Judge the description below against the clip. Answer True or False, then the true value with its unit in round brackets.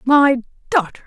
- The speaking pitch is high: True (255 Hz)